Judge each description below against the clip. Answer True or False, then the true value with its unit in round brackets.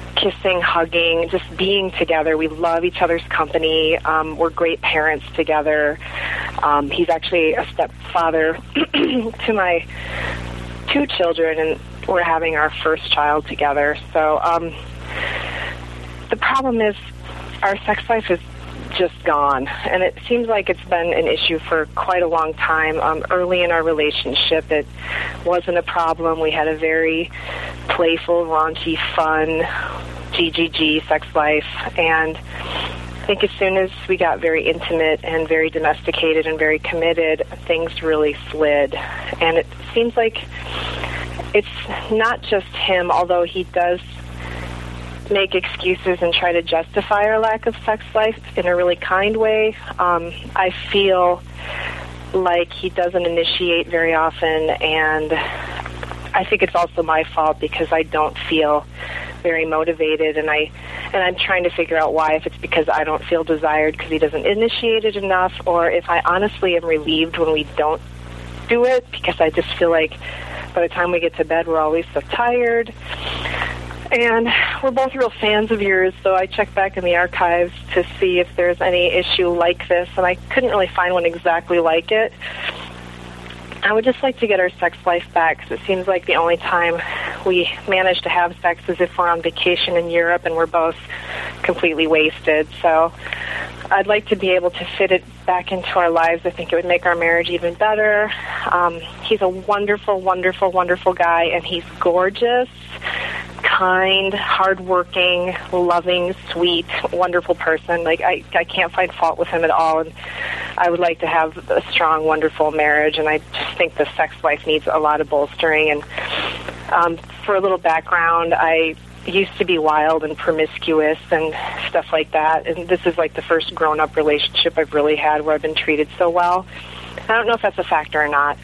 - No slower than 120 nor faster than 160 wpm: False (175 wpm)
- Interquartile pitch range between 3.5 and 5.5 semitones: False (2.8 semitones)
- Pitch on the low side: False (165 Hz)